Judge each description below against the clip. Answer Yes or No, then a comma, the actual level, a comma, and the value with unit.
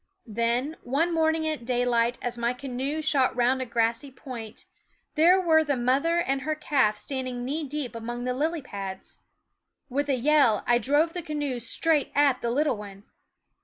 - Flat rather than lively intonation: No, average, 4.0 semitones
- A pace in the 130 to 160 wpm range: No, average, 170 wpm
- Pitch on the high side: Yes, very high, 260 Hz